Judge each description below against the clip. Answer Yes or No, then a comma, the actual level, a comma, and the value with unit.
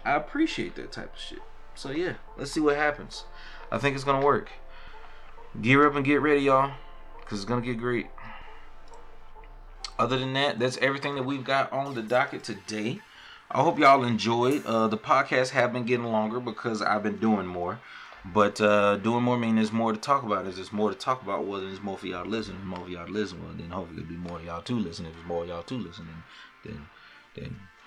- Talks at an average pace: No, fast, 215 wpm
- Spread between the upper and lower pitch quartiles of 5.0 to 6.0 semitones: Yes, average, 5.3 semitones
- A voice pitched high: No, low, 115 Hz